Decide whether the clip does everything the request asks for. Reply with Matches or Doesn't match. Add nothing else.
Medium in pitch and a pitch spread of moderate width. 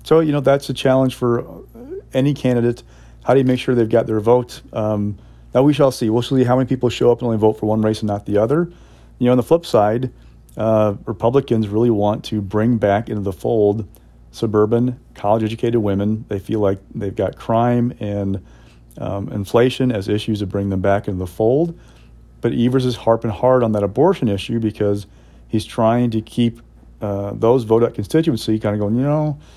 Doesn't match